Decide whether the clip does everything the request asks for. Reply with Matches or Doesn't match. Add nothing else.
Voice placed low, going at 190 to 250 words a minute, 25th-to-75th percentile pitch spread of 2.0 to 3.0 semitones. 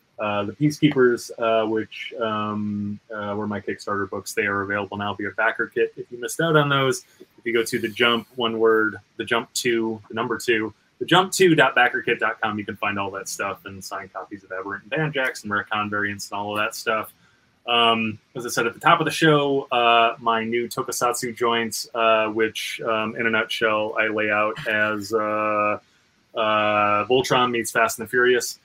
Matches